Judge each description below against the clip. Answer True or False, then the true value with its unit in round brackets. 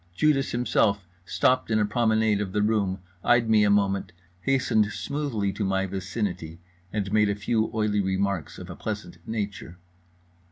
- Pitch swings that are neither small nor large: False (2.3 semitones)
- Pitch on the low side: True (105 Hz)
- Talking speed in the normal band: True (160 wpm)